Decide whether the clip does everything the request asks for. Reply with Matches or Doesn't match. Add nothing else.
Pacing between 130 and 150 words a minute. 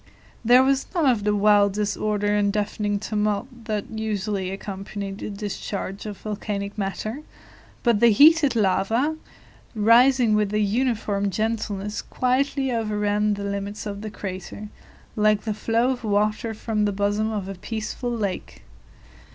Matches